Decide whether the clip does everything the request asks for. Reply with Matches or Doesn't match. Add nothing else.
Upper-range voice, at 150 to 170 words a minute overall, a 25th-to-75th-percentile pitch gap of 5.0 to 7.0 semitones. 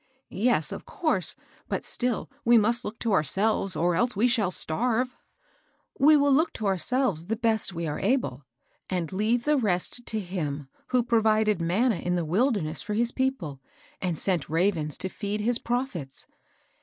Doesn't match